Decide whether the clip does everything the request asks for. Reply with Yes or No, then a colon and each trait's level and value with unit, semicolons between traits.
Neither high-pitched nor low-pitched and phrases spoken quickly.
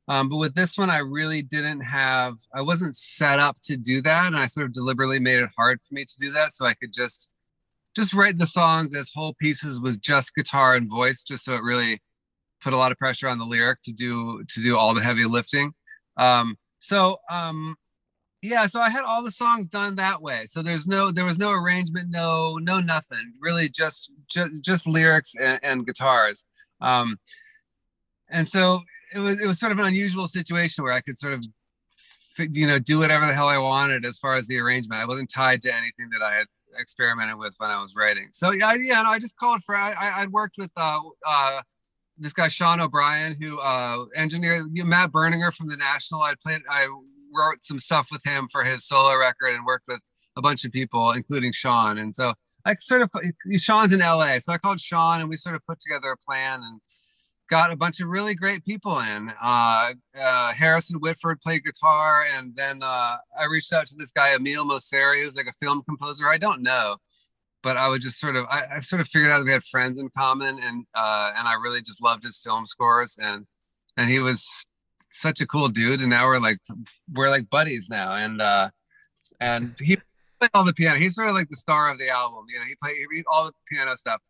Yes: medium, 145 Hz; fast, 225 wpm